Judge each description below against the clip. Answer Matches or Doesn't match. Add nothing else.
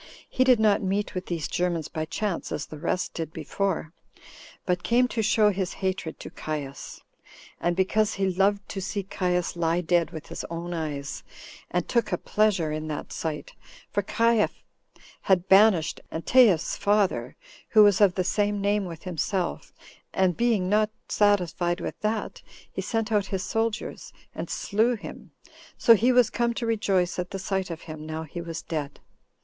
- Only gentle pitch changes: Doesn't match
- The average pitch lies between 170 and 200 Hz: Matches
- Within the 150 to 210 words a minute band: Matches